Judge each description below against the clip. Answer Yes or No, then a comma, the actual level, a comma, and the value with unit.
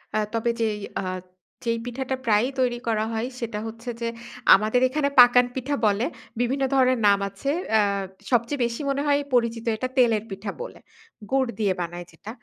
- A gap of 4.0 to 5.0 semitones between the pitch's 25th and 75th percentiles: No, average, 2.9 semitones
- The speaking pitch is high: Yes, high, 235 Hz